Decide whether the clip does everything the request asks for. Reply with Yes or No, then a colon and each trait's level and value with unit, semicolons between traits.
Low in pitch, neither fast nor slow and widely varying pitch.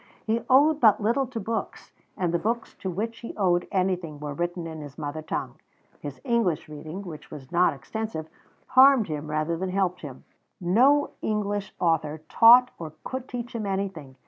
No: medium, 185 Hz; average, 175 wpm; wide, 6.5 semitones